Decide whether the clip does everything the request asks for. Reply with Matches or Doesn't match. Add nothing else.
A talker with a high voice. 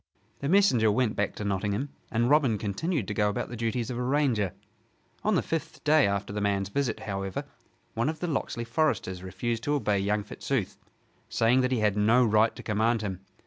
Doesn't match